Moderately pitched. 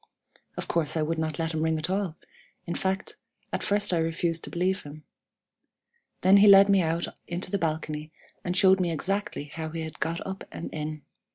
Yes: medium, 165 Hz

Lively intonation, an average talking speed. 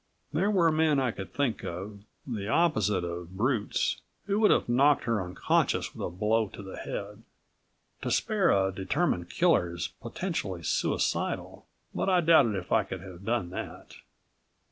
Yes: wide, 8.3 semitones; average, 165 wpm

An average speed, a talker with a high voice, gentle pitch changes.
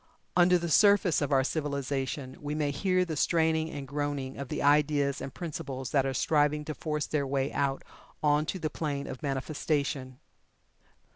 No: average, 170 wpm; medium, 145 Hz; narrow, 2.1 semitones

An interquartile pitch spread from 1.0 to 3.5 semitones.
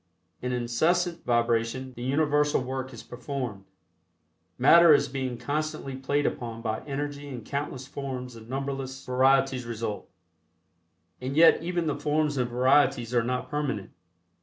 Yes: average, 3.0 semitones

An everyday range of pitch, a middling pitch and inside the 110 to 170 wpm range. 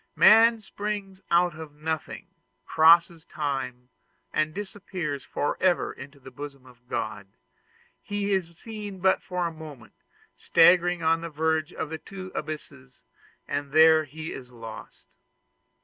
Yes: average, 4.2 semitones; medium, 160 Hz; slow, 135 wpm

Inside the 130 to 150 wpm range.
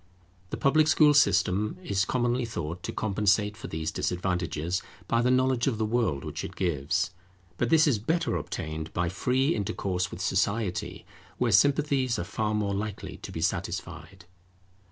No: average, 160 wpm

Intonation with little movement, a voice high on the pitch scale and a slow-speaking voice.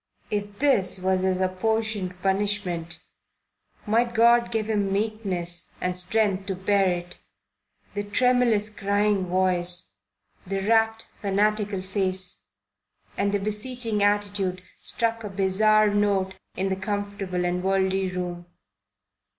Yes: narrow, 2.3 semitones; high, 200 Hz; slow, 120 wpm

